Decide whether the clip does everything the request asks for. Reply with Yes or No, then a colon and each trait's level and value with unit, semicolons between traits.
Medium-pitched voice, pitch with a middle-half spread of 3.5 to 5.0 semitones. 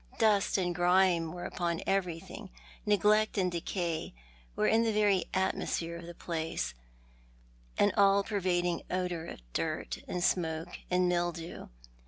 No: medium, 180 Hz; narrow, 2.5 semitones